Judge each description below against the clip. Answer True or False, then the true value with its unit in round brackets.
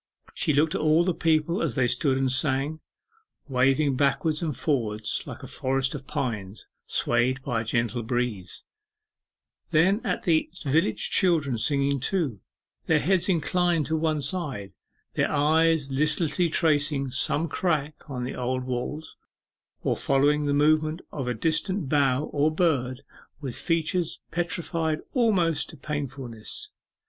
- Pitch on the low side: False (145 Hz)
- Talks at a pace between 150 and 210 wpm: False (140 wpm)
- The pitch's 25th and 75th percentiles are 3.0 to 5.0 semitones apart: True (3.7 semitones)